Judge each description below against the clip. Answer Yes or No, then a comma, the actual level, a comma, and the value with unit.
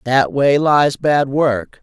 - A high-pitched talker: No, medium, 145 Hz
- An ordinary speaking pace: Yes, average, 165 wpm